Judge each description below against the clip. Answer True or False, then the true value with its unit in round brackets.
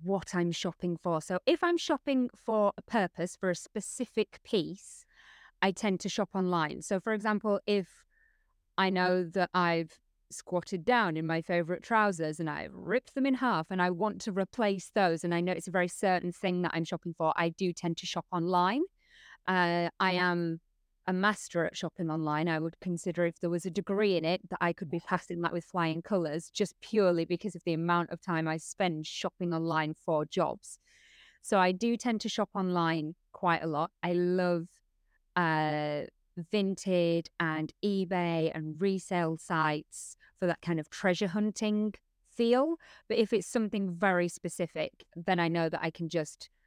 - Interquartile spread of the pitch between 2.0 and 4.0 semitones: True (3.1 semitones)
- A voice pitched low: False (180 Hz)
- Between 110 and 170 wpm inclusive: False (185 wpm)